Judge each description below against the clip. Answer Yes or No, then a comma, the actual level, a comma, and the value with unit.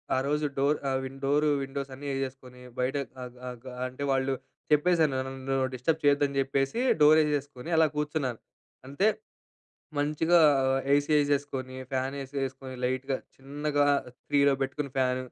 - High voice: No, low, 135 Hz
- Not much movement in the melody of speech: Yes, narrow, 1.9 semitones